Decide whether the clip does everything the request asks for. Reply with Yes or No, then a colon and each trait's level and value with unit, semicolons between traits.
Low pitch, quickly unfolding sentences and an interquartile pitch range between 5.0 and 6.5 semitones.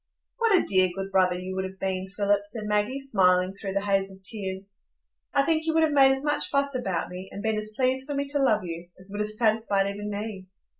No: high, 205 Hz; fast, 245 wpm; wide, 5.5 semitones